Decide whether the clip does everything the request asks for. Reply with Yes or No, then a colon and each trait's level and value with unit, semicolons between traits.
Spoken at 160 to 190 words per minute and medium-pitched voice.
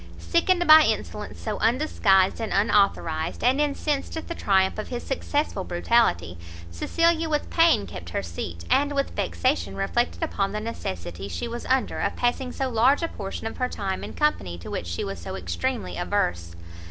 No: average, 175 wpm; high, 220 Hz